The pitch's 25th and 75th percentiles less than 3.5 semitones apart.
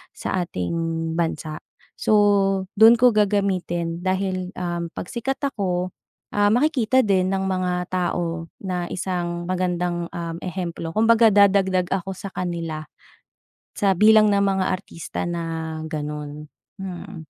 Yes: average, 2.7 semitones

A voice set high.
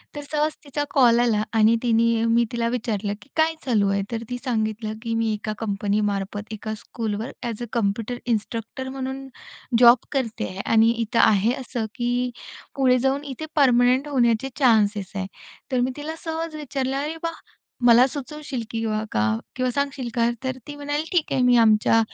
Yes: high, 240 Hz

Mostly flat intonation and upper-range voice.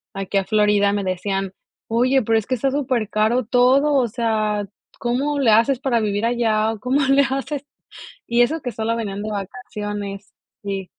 No: average, 3.6 semitones; high, 225 Hz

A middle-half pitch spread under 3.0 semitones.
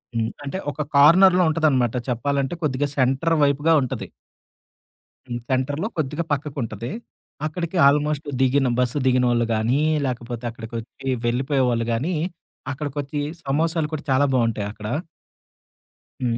No: average, 3.7 semitones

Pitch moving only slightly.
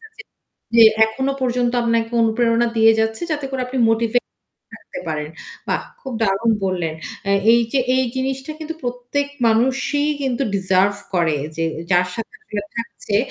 No: average, 4.3 semitones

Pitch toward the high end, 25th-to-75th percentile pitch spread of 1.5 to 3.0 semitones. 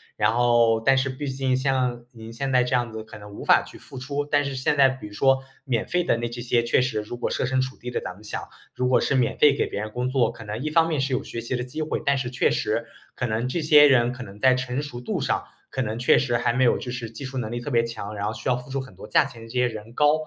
No: low, 125 Hz; narrow, 2.4 semitones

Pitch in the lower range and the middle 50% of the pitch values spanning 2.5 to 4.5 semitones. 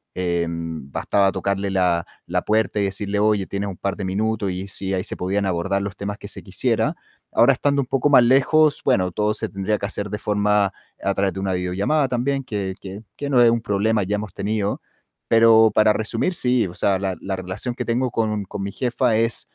Yes: low, 105 Hz; average, 2.9 semitones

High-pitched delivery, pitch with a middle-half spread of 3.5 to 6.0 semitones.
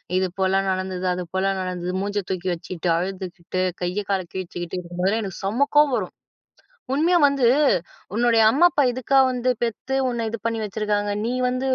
Yes: high, 195 Hz; average, 4.5 semitones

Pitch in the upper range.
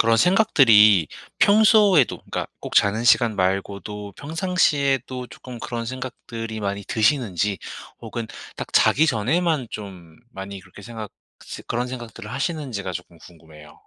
No: low, 115 Hz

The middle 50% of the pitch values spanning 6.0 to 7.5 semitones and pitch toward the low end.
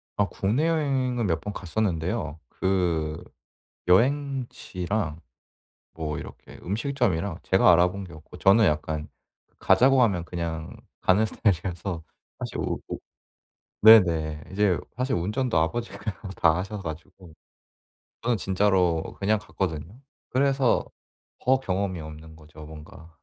No: average, 5.2 semitones; very low, 95 Hz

